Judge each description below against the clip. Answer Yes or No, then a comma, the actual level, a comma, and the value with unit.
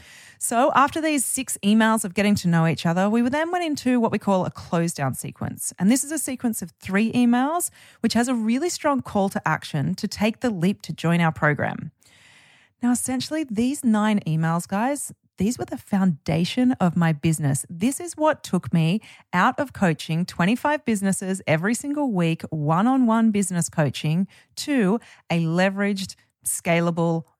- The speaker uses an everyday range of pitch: No, wide, 6.6 semitones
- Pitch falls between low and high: No, high, 200 Hz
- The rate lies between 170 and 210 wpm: Yes, average, 175 wpm